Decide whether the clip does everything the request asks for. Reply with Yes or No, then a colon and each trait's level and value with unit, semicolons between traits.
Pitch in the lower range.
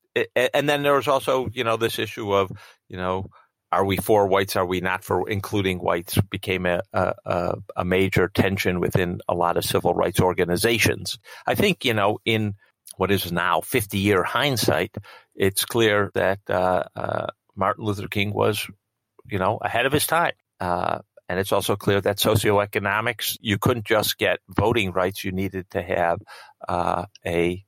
Yes: low, 100 Hz